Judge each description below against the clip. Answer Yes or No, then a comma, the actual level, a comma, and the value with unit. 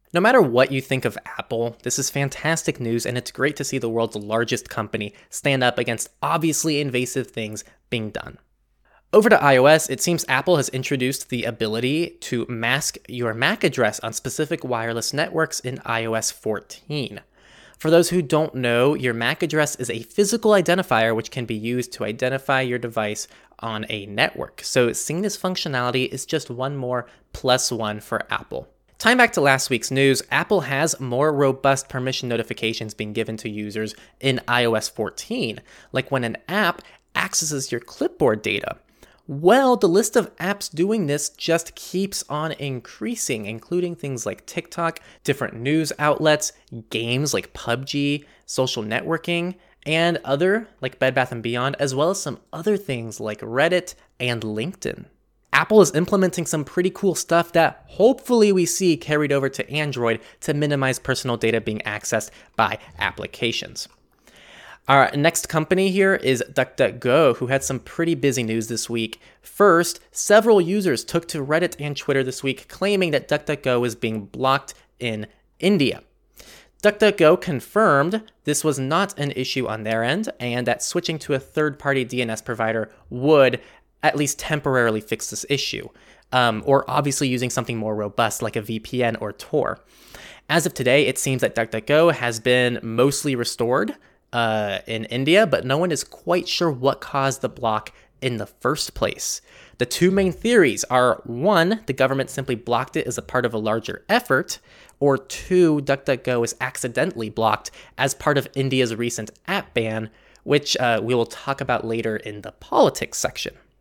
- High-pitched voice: No, low, 130 Hz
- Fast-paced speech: No, average, 165 wpm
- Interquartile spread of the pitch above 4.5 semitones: Yes, average, 5.1 semitones